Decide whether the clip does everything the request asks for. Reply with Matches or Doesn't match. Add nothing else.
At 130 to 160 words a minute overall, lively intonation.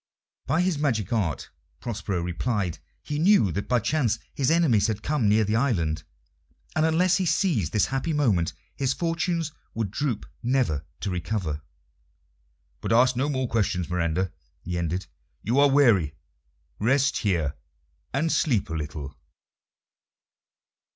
Matches